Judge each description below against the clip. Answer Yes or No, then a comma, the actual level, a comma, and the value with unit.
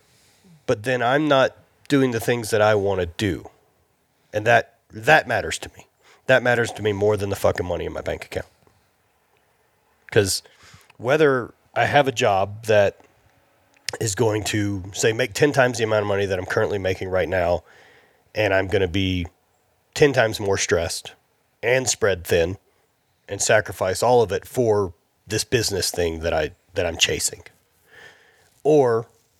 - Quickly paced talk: No, average, 165 wpm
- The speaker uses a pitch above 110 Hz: No, low, 105 Hz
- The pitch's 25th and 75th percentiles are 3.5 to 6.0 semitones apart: Yes, average, 3.8 semitones